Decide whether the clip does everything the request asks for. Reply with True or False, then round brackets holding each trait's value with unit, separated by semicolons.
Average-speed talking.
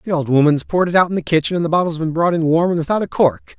False (335 wpm)